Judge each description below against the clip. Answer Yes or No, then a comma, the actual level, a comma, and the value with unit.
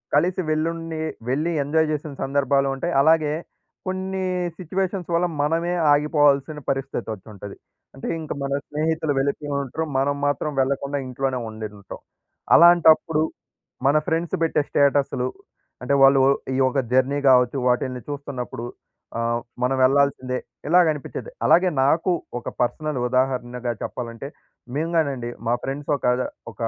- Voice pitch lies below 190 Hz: Yes, medium, 140 Hz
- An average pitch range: Yes, average, 3.5 semitones